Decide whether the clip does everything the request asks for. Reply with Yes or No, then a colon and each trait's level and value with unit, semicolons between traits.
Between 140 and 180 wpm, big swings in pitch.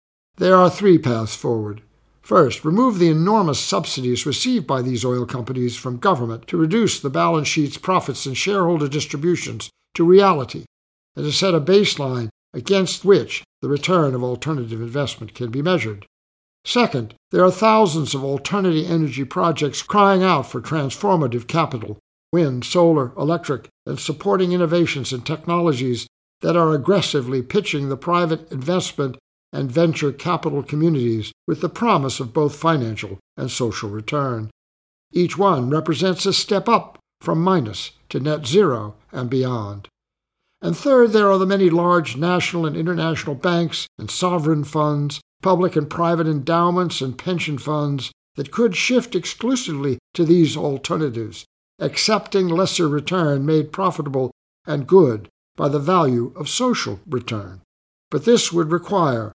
Yes: average, 145 wpm; wide, 5.9 semitones